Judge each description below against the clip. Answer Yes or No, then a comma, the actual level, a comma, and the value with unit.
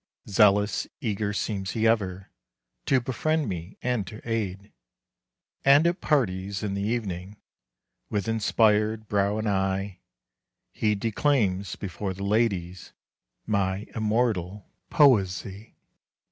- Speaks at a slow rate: Yes, slow, 110 wpm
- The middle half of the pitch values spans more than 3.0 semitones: No, average, 2.7 semitones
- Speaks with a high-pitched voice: No, low, 105 Hz